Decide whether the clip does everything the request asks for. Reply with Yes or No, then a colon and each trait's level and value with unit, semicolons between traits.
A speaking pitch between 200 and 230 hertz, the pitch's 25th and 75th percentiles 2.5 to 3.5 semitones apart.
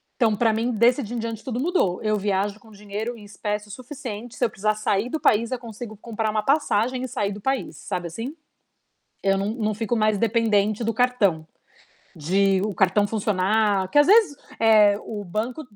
Yes: high, 215 Hz; average, 2.9 semitones